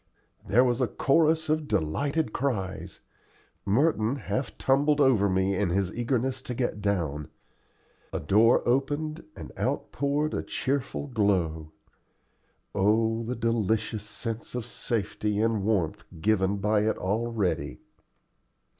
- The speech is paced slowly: Yes, slow, 125 wpm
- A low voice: Yes, low, 115 Hz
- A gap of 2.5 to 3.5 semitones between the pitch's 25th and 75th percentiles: No, average, 4.8 semitones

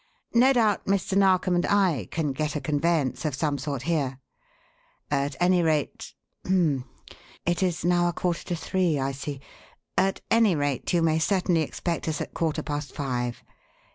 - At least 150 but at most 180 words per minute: Yes, average, 170 wpm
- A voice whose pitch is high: No, medium, 160 Hz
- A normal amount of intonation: Yes, average, 4.0 semitones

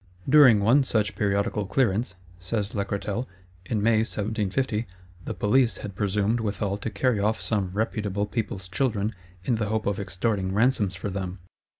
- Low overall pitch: Yes, low, 105 Hz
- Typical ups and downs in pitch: No, narrow, 2.2 semitones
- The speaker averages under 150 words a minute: No, average, 155 wpm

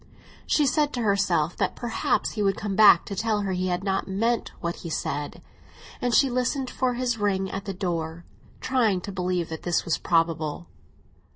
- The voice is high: Yes, high, 195 Hz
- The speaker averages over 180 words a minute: Yes, average, 190 wpm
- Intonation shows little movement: No, average, 4.9 semitones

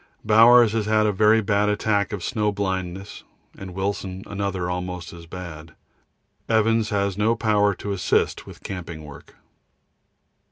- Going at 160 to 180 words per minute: No, average, 145 wpm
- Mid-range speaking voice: No, low, 100 Hz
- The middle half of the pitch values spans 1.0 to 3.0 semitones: Yes, average, 2.7 semitones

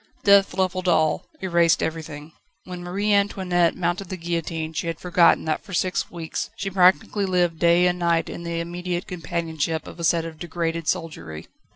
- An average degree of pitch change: No, narrow, 1.8 semitones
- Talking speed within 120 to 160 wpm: No, average, 175 wpm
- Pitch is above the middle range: No, medium, 170 Hz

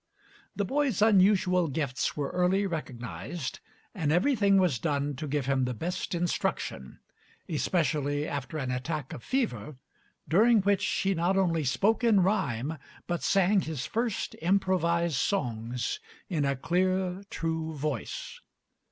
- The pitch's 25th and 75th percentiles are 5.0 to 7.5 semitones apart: Yes, average, 5.3 semitones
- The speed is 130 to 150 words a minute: Yes, slow, 135 wpm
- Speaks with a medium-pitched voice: Yes, medium, 170 Hz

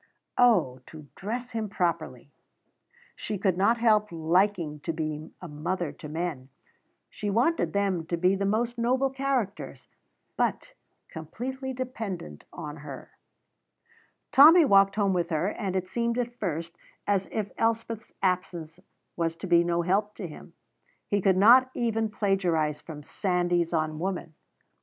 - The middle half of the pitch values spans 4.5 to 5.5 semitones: Yes, average, 5.2 semitones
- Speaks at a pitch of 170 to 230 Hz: Yes, high, 190 Hz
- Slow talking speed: No, average, 145 wpm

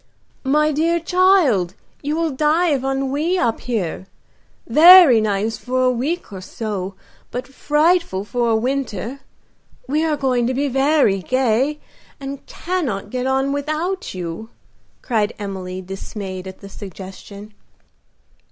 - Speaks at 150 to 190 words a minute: No, slow, 135 wpm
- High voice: Yes, very high, 255 Hz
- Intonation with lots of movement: Yes, wide, 6.7 semitones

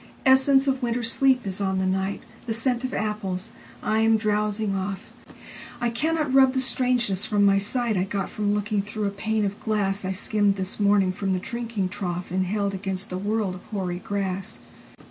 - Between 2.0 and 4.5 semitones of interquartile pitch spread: Yes, average, 3.1 semitones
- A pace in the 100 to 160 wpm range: No, average, 175 wpm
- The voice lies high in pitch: Yes, high, 205 Hz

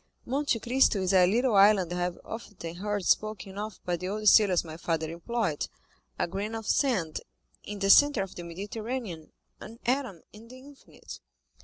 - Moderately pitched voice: No, high, 205 Hz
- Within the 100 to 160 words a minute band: No, average, 170 wpm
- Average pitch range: Yes, average, 4.5 semitones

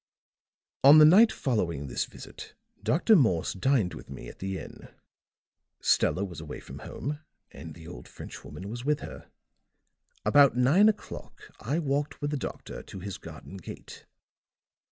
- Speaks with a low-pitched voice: Yes, low, 120 Hz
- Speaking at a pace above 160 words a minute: No, average, 155 wpm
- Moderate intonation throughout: No, wide, 8.6 semitones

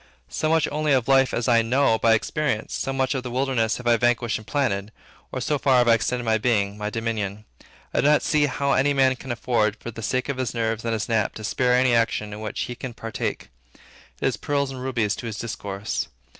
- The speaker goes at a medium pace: No, fast, 240 wpm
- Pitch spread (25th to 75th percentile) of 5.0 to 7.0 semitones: No, average, 3.0 semitones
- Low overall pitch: Yes, low, 120 Hz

